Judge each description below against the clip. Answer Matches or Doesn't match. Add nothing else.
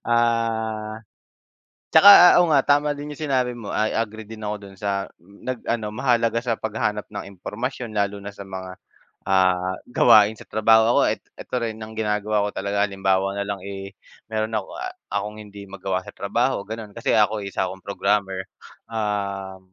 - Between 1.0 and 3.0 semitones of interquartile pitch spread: Matches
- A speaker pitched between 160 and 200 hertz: Doesn't match